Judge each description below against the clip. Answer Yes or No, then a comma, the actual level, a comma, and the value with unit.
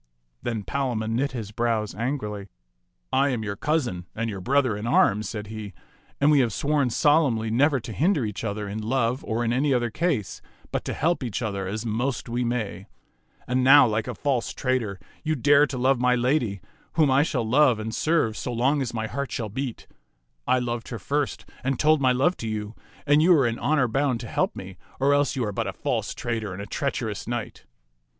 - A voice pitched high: No, low, 120 Hz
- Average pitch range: Yes, average, 4.3 semitones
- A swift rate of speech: Yes, fast, 225 wpm